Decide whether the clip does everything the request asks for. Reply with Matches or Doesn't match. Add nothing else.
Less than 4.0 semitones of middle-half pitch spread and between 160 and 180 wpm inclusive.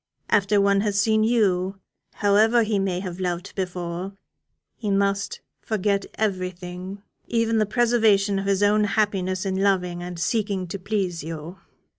Doesn't match